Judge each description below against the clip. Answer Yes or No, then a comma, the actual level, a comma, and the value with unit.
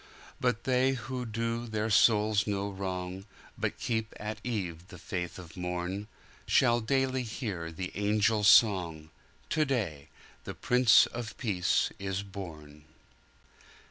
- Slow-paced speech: Yes, slow, 115 wpm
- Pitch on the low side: Yes, low, 105 Hz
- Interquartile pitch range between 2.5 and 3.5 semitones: No, average, 4.3 semitones